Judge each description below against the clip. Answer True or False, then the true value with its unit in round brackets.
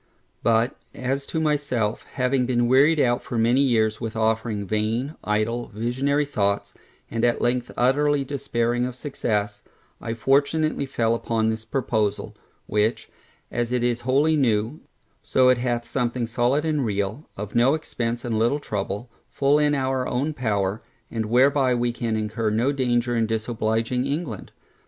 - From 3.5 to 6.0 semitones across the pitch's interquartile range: False (3.1 semitones)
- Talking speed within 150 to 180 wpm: True (155 wpm)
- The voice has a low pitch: True (120 Hz)